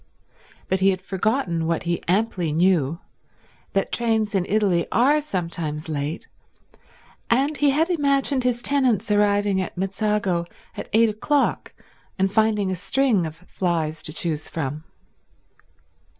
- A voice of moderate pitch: No, high, 195 Hz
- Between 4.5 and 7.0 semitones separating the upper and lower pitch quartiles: Yes, average, 5.2 semitones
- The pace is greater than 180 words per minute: No, slow, 135 wpm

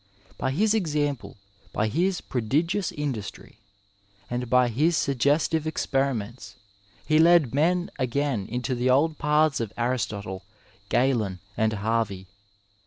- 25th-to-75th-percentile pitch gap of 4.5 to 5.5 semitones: Yes, average, 5.1 semitones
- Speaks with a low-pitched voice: Yes, low, 130 Hz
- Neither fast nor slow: No, slow, 115 wpm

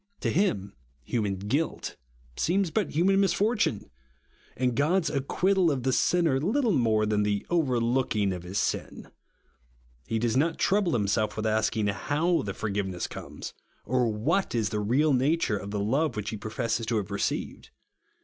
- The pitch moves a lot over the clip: Yes, wide, 7.6 semitones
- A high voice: No, low, 120 Hz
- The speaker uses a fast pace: No, average, 165 wpm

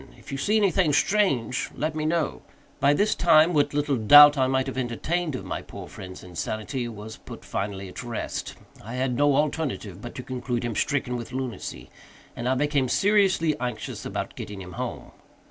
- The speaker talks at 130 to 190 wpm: Yes, average, 185 wpm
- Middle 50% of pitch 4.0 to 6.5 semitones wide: Yes, average, 4.4 semitones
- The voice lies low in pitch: Yes, low, 130 Hz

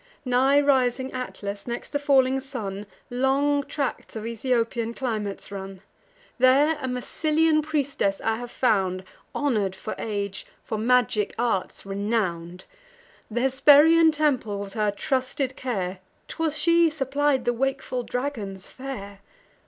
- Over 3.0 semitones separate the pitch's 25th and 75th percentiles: Yes, average, 5.2 semitones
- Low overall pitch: No, very high, 250 Hz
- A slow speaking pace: Yes, slow, 125 wpm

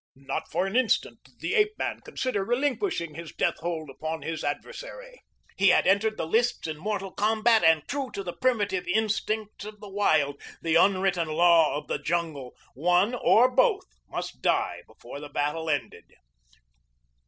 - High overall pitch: Yes, high, 195 Hz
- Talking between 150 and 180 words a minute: Yes, average, 165 wpm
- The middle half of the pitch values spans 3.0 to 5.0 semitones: No, wide, 5.6 semitones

